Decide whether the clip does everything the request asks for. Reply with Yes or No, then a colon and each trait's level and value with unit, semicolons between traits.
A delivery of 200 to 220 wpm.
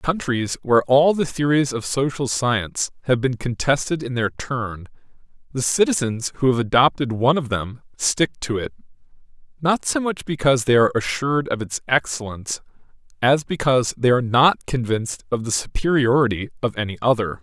No: average, 165 wpm